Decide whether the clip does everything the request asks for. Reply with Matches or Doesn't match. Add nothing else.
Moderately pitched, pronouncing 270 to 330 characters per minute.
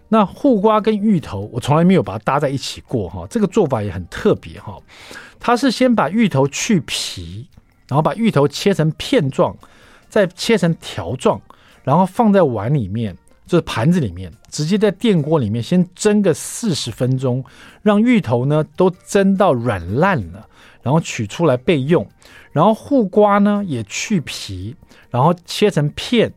Doesn't match